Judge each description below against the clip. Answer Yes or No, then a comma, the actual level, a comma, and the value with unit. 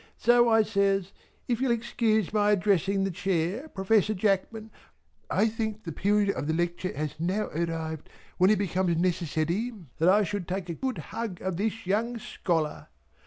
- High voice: Yes, high, 195 Hz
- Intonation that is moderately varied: Yes, average, 3.9 semitones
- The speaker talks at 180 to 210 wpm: No, average, 165 wpm